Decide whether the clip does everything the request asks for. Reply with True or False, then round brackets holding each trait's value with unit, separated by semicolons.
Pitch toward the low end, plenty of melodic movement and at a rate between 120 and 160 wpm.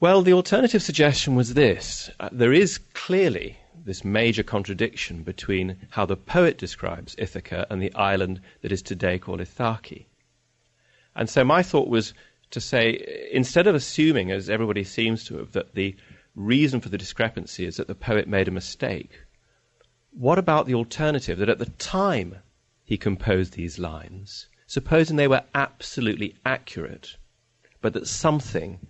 True (110 Hz; 6.5 semitones; 155 wpm)